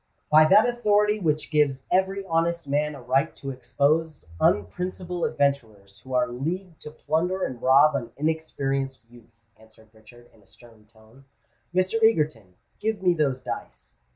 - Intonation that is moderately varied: No, wide, 6.1 semitones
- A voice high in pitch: No, medium, 145 Hz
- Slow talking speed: No, average, 155 wpm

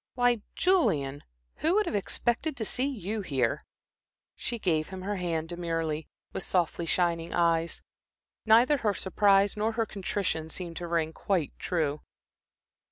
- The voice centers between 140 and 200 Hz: Yes, medium, 185 Hz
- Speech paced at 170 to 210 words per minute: No, average, 145 wpm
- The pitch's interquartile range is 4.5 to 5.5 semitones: Yes, average, 5.1 semitones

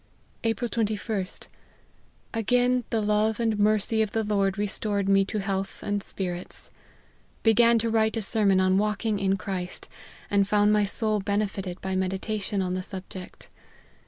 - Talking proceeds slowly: No, average, 160 wpm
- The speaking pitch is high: Yes, high, 205 Hz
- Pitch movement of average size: No, narrow, 2.1 semitones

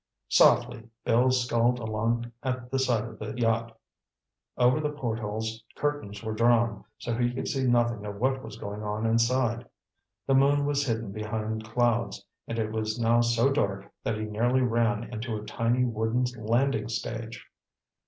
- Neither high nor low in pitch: No, low, 115 Hz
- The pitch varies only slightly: Yes, narrow, 2.0 semitones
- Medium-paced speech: Yes, average, 165 wpm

